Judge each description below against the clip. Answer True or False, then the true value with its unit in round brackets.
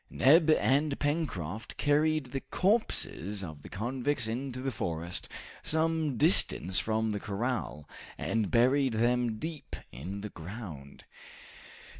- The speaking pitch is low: True (120 Hz)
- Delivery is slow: True (120 wpm)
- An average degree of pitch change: False (6.5 semitones)